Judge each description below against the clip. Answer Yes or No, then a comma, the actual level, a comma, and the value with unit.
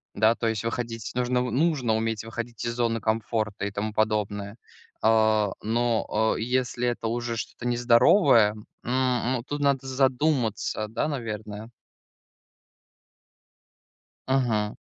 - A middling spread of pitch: No, narrow, 2.2 semitones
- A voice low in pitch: Yes, low, 115 Hz